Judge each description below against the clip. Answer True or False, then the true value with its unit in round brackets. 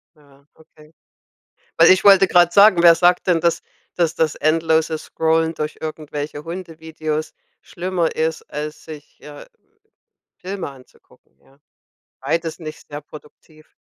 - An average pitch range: False (2.0 semitones)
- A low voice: False (160 Hz)